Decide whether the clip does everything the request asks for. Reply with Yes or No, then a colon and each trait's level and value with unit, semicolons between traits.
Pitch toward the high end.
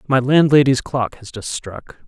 No: low, 130 Hz